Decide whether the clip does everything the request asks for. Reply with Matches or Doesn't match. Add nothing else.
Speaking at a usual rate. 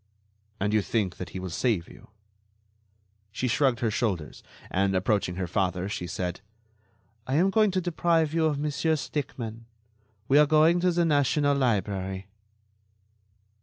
Matches